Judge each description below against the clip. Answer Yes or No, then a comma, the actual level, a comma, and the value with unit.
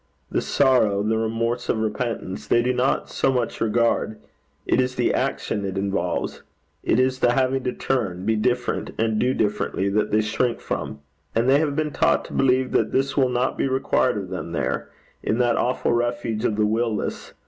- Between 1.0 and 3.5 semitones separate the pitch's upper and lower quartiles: Yes, average, 2.9 semitones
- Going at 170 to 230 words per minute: Yes, average, 195 wpm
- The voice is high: No, low, 120 Hz